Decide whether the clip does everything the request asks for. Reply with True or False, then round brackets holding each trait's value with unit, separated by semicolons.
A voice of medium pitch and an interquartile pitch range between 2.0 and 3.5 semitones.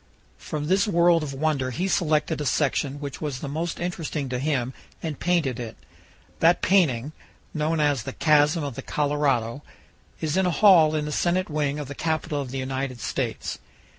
True (150 Hz; 3.2 semitones)